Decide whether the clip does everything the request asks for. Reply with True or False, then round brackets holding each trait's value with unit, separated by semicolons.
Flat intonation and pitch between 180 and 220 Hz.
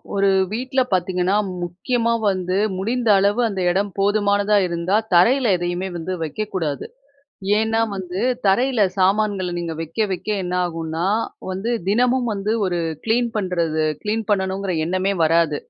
False (3.4 semitones; 195 Hz)